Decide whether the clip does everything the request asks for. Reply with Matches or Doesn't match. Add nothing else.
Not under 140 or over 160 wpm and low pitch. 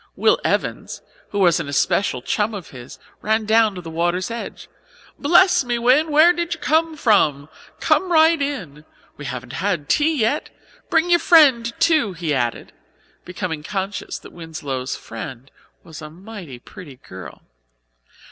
Doesn't match